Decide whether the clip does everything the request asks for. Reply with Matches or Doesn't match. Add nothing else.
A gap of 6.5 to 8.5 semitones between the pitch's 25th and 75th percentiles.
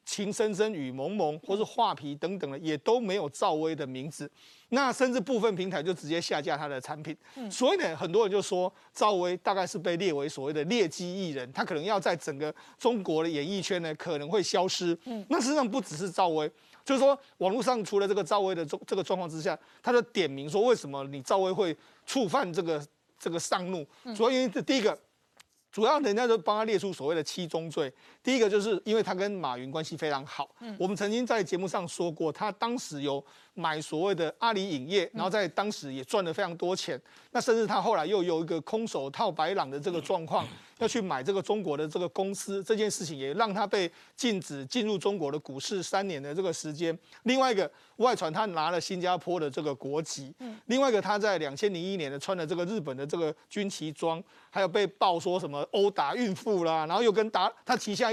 Doesn't match